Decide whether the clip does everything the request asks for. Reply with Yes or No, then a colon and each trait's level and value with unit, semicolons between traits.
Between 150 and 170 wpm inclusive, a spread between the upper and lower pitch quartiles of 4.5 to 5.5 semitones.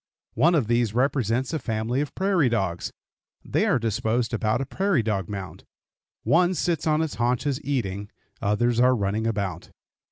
Yes: average, 160 wpm; average, 5.0 semitones